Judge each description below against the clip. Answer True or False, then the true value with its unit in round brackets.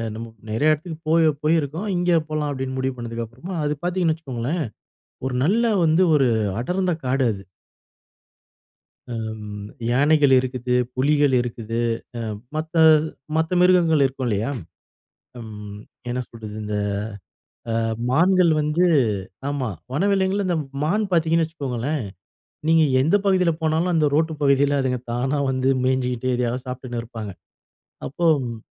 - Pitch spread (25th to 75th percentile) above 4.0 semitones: True (4.8 semitones)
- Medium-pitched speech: True (145 Hz)